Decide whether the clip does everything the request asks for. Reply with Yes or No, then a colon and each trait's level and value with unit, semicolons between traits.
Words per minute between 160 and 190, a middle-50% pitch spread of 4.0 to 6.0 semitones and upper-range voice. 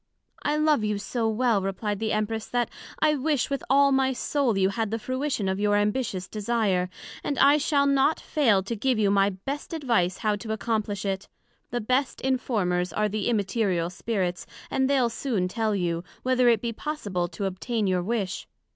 Yes: average, 185 wpm; average, 4.8 semitones; high, 220 Hz